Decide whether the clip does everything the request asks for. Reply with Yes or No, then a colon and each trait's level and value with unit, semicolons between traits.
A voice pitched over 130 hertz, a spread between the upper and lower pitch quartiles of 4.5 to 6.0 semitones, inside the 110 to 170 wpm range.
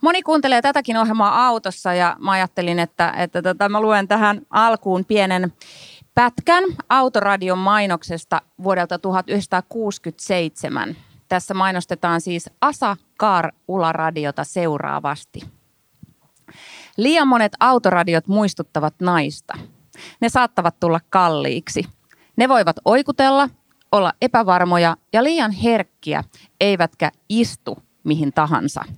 No: high, 190 Hz; average, 4.9 semitones; average, 100 wpm